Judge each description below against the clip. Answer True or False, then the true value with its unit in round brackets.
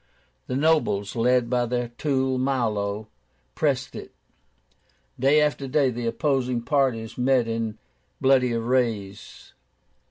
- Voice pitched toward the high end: False (125 Hz)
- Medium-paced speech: False (115 wpm)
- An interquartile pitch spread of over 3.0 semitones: False (2.7 semitones)